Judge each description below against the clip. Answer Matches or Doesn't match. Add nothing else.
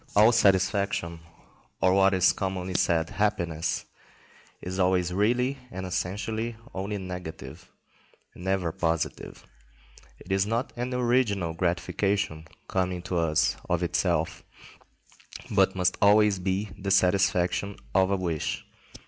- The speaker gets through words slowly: Matches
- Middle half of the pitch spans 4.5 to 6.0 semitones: Doesn't match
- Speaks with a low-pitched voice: Matches